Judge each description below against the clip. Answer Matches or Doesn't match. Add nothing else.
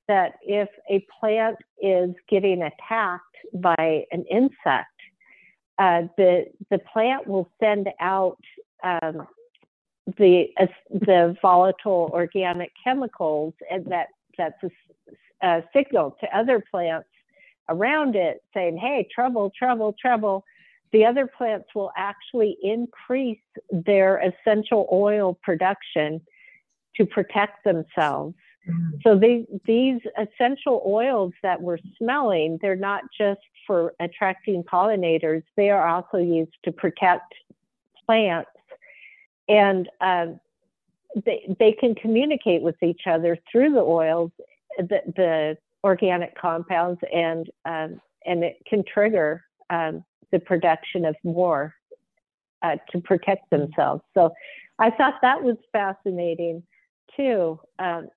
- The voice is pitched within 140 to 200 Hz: Matches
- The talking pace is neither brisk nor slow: Doesn't match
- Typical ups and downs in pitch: Matches